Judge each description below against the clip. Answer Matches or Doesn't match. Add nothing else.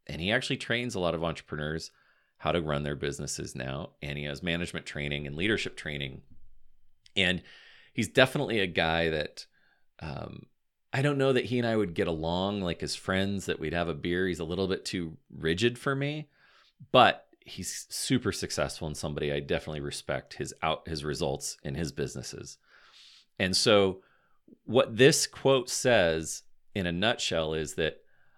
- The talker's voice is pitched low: Matches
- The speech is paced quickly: Doesn't match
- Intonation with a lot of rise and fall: Matches